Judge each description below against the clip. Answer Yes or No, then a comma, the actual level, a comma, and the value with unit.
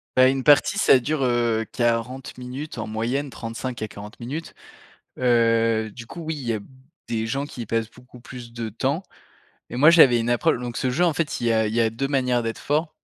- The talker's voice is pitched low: Yes, low, 120 Hz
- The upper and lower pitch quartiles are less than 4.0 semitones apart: Yes, average, 2.8 semitones